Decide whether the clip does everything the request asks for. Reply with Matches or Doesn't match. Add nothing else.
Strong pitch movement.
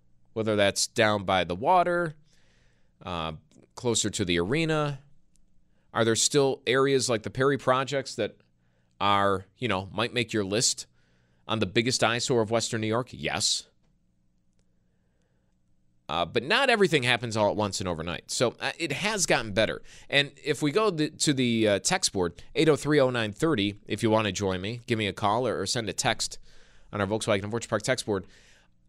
Matches